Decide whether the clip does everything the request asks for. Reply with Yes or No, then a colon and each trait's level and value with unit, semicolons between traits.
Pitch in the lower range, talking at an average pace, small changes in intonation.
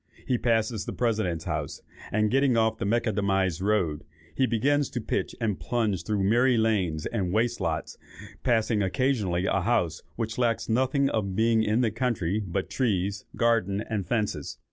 No: low, 110 Hz; average, 160 wpm; average, 3.5 semitones